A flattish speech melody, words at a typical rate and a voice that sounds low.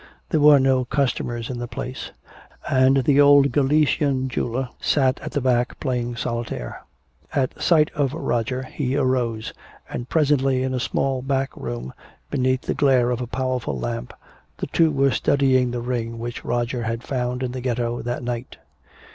Yes: narrow, 2.1 semitones; average, 165 wpm; low, 130 Hz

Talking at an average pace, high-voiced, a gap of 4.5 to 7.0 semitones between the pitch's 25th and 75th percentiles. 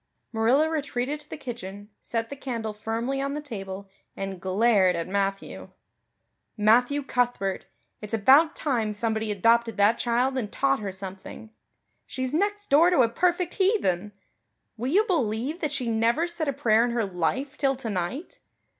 Yes: average, 160 wpm; high, 235 Hz; average, 5.2 semitones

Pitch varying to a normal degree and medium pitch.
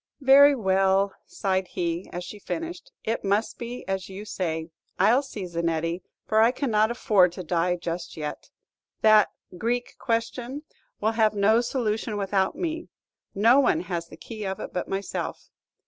No: average, 4.5 semitones; high, 205 Hz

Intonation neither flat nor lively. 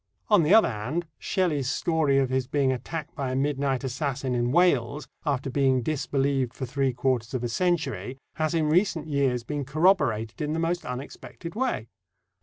Yes: average, 3.7 semitones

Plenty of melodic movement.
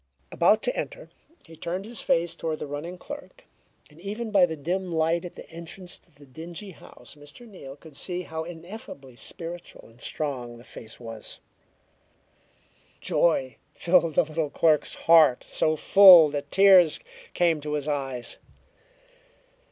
No: average, 3.6 semitones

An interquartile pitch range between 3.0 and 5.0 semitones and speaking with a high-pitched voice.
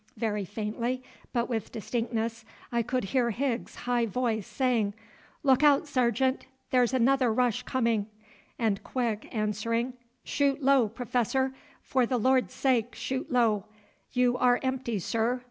No: narrow, 2.5 semitones; high, 245 Hz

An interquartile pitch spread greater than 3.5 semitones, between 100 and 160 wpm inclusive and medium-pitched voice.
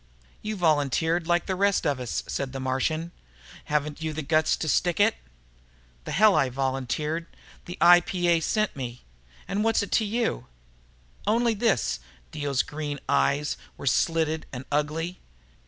Yes: average, 4.2 semitones; average, 150 wpm; medium, 160 Hz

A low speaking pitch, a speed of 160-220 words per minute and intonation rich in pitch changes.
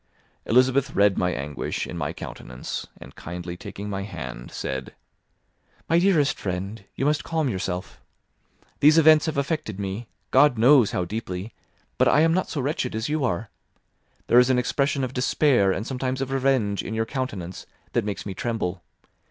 Yes: low, 120 Hz; average, 170 wpm; wide, 6.2 semitones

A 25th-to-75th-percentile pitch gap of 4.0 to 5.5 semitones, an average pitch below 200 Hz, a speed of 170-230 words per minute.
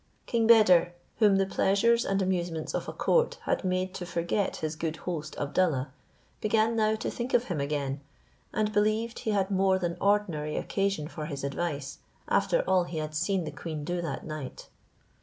Yes: average, 5.1 semitones; medium, 185 Hz; average, 180 wpm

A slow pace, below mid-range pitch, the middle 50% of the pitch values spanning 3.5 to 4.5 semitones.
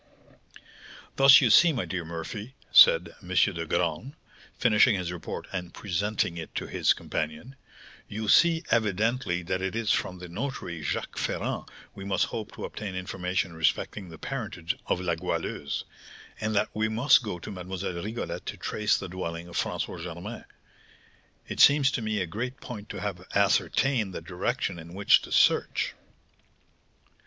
No: average, 160 wpm; very low, 95 Hz; average, 4.0 semitones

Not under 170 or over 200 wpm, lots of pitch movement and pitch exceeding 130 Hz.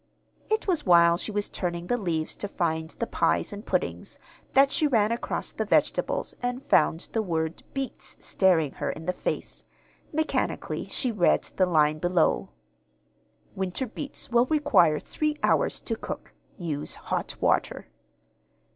No: average, 150 wpm; wide, 6.7 semitones; high, 190 Hz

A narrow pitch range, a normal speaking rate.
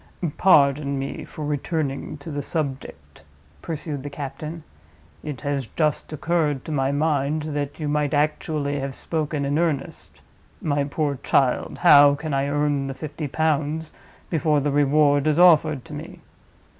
Yes: narrow, 1.7 semitones; average, 150 wpm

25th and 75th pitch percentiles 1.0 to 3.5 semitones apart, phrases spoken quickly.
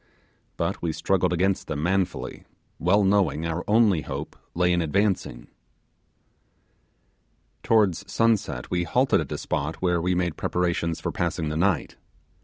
No: average, 2.8 semitones; average, 140 wpm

